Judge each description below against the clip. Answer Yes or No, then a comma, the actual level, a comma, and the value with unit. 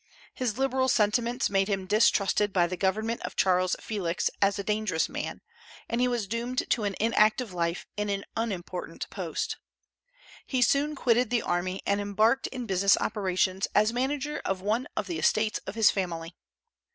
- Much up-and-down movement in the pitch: No, average, 3.7 semitones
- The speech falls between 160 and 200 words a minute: Yes, average, 170 wpm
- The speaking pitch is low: No, high, 210 Hz